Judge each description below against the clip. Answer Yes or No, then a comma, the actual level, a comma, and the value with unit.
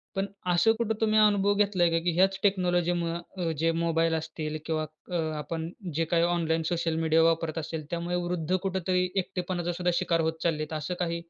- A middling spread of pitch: No, narrow, 1.9 semitones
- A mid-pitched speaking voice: Yes, medium, 170 Hz